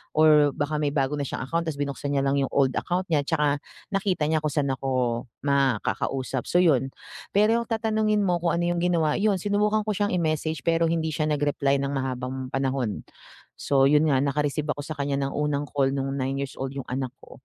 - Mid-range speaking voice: Yes, medium, 145 Hz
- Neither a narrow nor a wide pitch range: Yes, average, 3.3 semitones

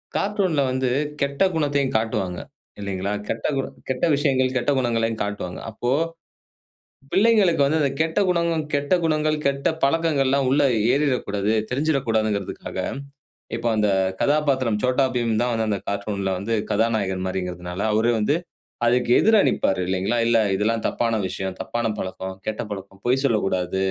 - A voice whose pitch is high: No, low, 120 Hz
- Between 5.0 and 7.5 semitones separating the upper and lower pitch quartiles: Yes, wide, 5.6 semitones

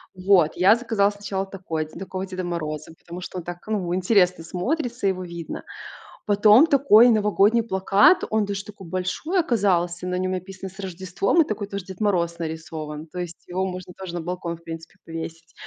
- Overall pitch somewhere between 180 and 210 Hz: Yes, medium, 185 Hz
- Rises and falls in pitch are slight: No, average, 3.0 semitones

